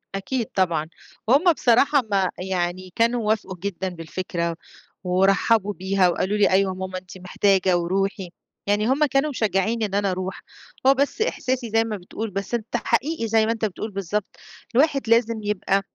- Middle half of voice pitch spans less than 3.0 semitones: No, average, 3.7 semitones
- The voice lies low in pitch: No, high, 200 Hz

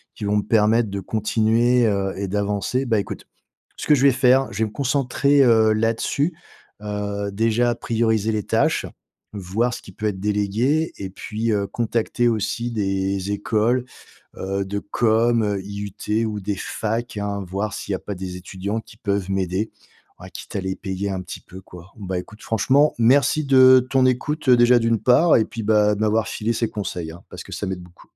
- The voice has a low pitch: Yes, low, 110 Hz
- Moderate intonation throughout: Yes, average, 3.1 semitones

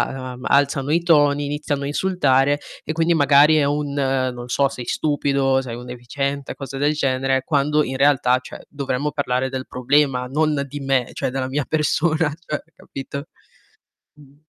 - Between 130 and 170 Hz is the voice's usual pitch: Yes, medium, 140 Hz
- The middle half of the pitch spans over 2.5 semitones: No, narrow, 1.9 semitones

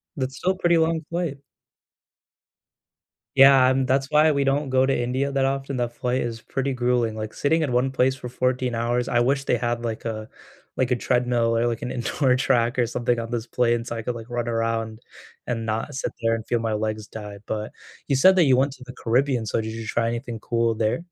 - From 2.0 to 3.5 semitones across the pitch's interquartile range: Yes, narrow, 2.6 semitones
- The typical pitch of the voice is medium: No, low, 125 Hz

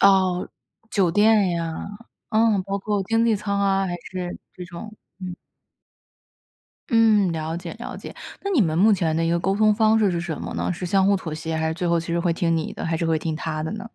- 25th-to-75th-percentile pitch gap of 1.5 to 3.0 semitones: No, average, 3.7 semitones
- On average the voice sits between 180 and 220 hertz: Yes, medium, 185 Hz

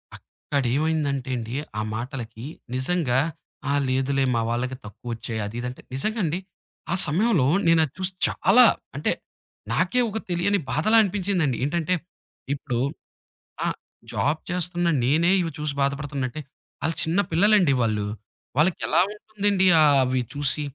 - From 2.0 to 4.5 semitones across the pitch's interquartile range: No, wide, 5.6 semitones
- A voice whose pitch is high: No, medium, 150 Hz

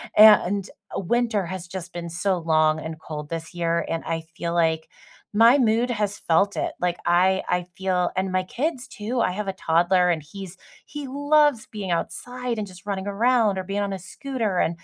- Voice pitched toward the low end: No, high, 190 Hz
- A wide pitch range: No, average, 4.2 semitones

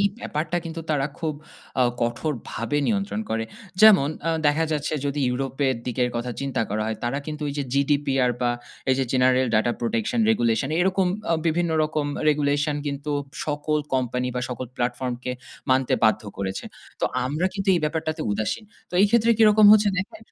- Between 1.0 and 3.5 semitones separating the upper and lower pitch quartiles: No, average, 4.4 semitones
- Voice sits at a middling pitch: Yes, medium, 145 Hz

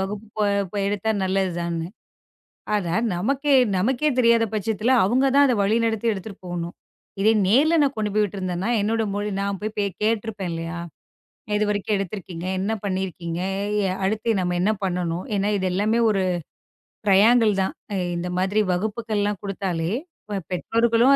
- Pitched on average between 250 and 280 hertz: No, high, 205 Hz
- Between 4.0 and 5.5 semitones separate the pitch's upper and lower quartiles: No, average, 3.2 semitones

